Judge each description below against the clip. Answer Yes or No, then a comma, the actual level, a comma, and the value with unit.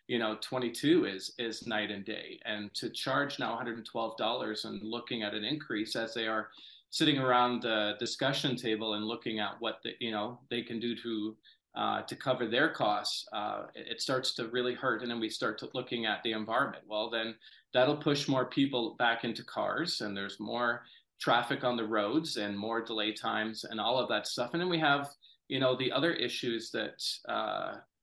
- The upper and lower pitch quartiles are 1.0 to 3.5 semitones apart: Yes, narrow, 2.6 semitones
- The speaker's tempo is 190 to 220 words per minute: Yes, average, 200 wpm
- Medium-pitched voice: No, low, 115 Hz